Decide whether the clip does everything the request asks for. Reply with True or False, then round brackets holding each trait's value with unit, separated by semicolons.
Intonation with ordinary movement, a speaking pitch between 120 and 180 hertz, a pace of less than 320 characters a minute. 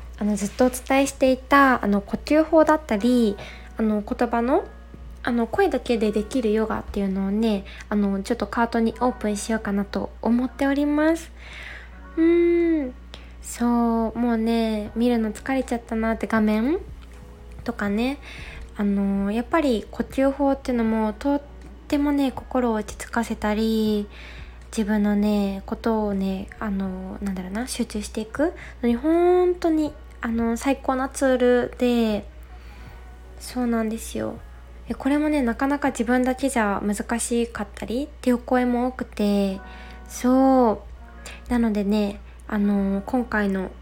False (3.8 semitones; 230 Hz; 285 characters per minute)